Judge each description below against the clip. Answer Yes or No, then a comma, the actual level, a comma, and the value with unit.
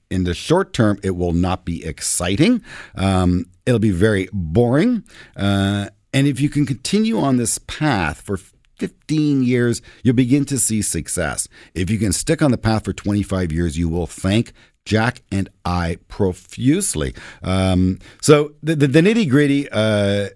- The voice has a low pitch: Yes, low, 105 Hz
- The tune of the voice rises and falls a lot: Yes, wide, 6.8 semitones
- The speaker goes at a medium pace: Yes, average, 165 wpm